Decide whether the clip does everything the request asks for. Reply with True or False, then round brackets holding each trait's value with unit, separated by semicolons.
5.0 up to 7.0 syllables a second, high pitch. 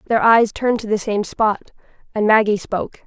True (5.5 syllables/s; 215 Hz)